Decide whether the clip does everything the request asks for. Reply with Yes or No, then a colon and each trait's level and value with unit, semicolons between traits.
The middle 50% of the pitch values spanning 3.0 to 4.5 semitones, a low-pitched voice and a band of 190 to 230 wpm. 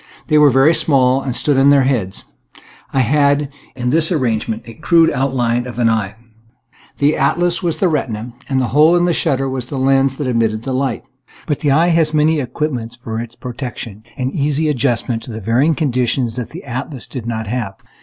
Yes: average, 3.8 semitones; low, 130 Hz; average, 195 wpm